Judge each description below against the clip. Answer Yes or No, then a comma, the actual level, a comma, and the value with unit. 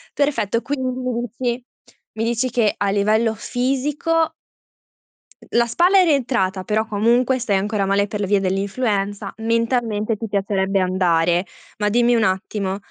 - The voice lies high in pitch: Yes, high, 220 Hz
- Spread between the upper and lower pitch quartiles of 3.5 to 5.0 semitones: Yes, average, 3.8 semitones